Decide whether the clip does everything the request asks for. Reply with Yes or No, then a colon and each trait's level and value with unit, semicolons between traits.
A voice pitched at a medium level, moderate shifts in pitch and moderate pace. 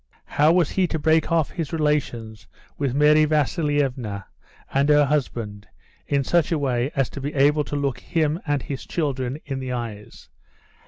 Yes: medium, 145 Hz; average, 3.0 semitones; average, 170 wpm